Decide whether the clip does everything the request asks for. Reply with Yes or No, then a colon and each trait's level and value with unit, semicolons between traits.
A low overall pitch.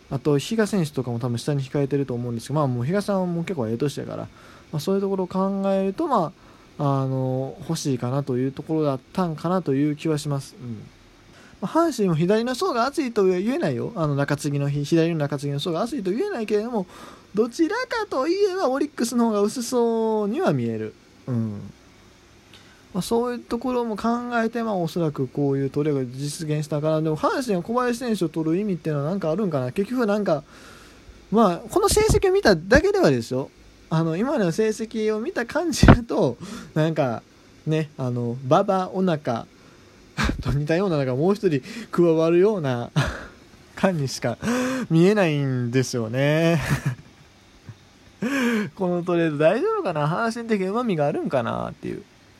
No: medium, 165 Hz